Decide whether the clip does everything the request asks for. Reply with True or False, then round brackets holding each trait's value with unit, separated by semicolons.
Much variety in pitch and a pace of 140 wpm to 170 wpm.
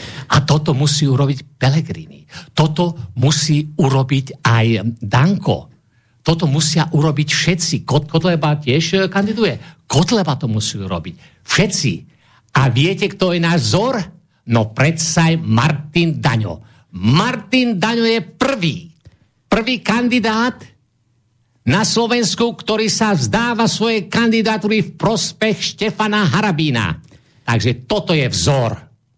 False (7.2 semitones; 110 wpm)